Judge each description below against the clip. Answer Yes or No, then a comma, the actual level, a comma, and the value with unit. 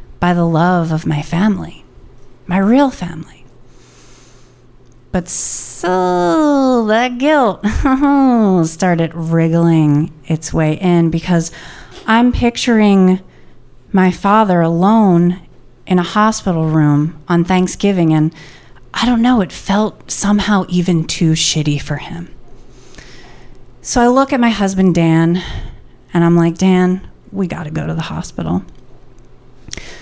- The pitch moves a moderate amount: Yes, average, 4.7 semitones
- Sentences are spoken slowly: Yes, slow, 120 wpm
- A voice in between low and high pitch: Yes, medium, 170 Hz